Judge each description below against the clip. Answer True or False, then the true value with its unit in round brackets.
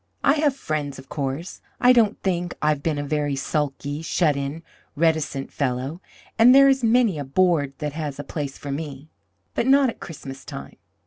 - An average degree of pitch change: True (4.9 semitones)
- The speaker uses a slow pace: False (180 wpm)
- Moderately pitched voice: True (150 Hz)